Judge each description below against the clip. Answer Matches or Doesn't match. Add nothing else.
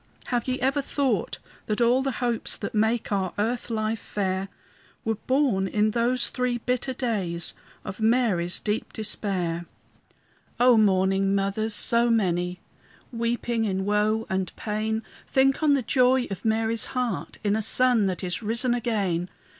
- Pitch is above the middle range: Matches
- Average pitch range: Matches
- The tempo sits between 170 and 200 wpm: Doesn't match